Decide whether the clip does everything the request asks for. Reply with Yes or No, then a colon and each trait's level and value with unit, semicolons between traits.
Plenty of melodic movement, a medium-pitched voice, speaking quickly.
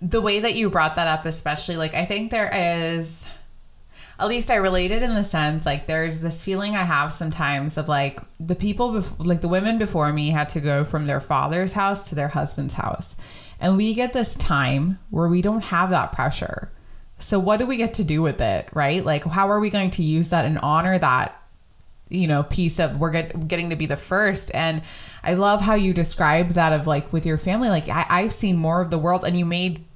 No: average, 4.0 semitones; medium, 170 Hz; fast, 230 wpm